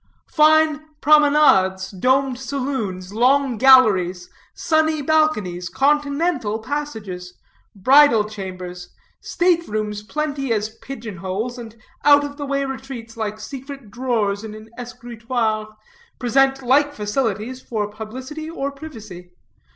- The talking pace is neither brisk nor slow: No, slow, 110 wpm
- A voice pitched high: Yes, high, 245 Hz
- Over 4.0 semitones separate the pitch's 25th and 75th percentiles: Yes, average, 5.2 semitones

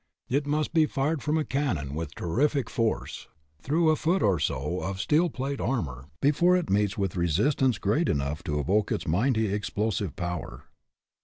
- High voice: No, low, 110 Hz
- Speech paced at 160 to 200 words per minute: Yes, average, 175 wpm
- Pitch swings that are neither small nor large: No, wide, 9.0 semitones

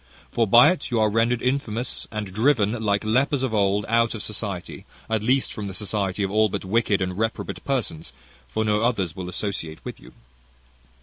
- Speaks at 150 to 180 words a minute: No, average, 190 wpm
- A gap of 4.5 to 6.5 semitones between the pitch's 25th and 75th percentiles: No, average, 2.9 semitones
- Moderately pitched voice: No, low, 110 Hz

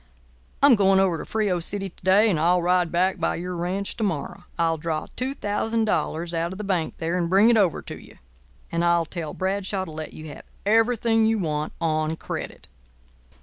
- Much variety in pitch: No, average, 3.6 semitones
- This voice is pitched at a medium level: Yes, medium, 180 Hz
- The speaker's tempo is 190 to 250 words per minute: Yes, average, 195 wpm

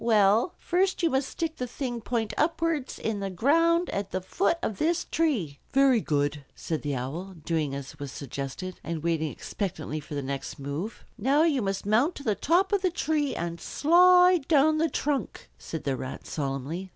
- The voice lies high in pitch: Yes, high, 215 Hz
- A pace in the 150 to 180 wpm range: No, average, 190 wpm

